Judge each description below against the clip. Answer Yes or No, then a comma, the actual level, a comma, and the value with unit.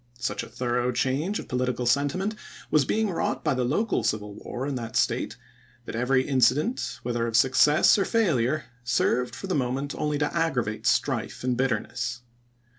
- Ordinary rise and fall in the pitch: Yes, average, 3.7 semitones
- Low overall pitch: Yes, low, 130 Hz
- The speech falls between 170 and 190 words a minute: Yes, average, 175 wpm